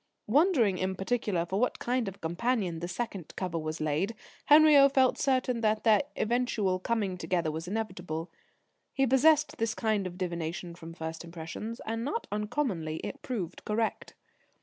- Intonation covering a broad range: Yes, wide, 5.9 semitones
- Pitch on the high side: Yes, high, 205 Hz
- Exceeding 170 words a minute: No, average, 160 wpm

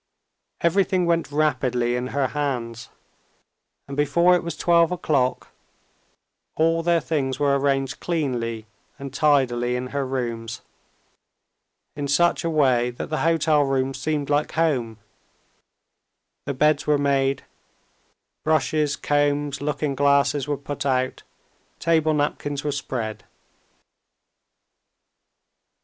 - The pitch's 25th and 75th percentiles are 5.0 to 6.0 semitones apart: No, average, 2.9 semitones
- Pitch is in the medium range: Yes, medium, 145 Hz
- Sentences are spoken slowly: Yes, slow, 115 wpm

